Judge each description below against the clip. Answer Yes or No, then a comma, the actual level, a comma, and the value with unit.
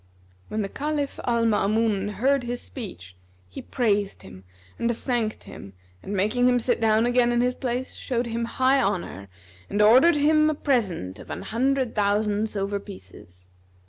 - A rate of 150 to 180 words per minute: Yes, average, 165 wpm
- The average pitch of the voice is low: No, high, 225 Hz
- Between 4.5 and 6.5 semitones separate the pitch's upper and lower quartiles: No, average, 3.7 semitones